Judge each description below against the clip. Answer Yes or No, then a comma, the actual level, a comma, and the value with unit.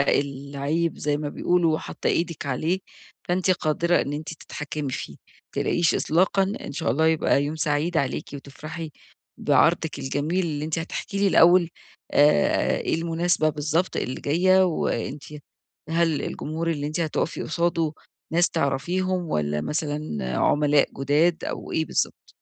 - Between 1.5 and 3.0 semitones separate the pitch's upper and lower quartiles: Yes, average, 2.7 semitones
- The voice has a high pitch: No, medium, 155 Hz